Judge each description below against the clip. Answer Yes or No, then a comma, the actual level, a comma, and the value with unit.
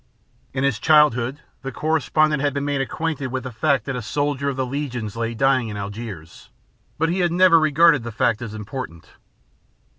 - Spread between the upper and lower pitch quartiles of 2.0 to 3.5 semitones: No, average, 4.3 semitones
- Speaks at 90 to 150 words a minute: No, average, 190 wpm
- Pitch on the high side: No, low, 135 Hz